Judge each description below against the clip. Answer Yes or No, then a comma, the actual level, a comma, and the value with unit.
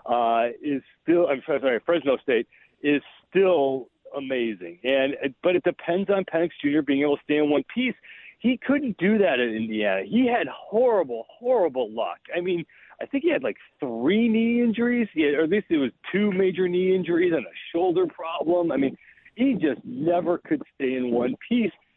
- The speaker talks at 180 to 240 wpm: Yes, average, 190 wpm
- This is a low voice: No, medium, 175 Hz